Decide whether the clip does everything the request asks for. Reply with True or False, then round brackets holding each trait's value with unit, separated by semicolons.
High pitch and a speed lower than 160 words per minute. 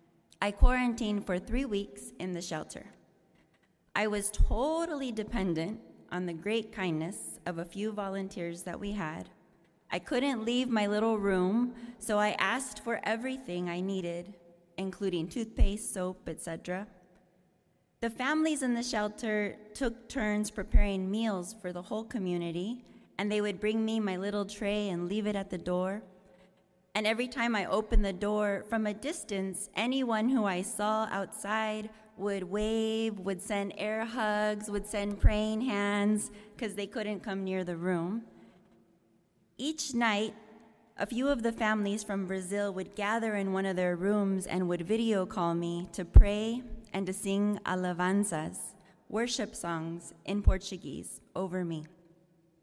True (205 Hz; 150 wpm)